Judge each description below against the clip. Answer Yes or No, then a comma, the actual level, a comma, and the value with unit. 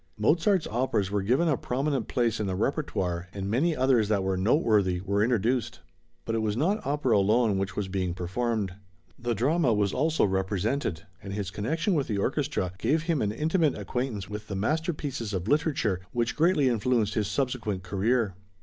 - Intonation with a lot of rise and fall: Yes, wide, 5.9 semitones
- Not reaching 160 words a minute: No, average, 175 wpm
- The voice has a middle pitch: No, low, 115 Hz